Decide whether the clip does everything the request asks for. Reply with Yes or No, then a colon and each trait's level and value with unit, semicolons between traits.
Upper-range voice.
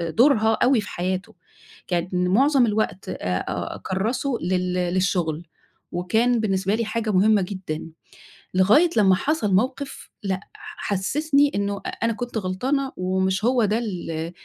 Yes: high, 205 Hz